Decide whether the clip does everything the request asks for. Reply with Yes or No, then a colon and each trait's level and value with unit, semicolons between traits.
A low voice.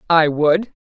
No: medium, 165 Hz